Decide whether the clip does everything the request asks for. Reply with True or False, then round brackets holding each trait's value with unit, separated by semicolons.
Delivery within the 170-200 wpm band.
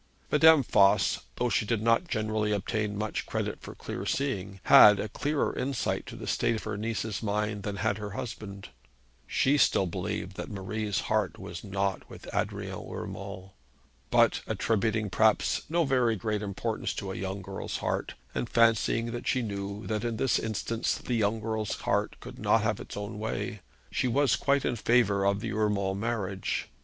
True (175 wpm)